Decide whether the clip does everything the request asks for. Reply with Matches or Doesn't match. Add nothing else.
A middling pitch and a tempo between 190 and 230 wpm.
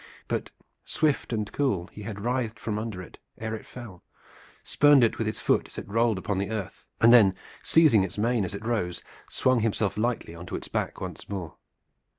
Doesn't match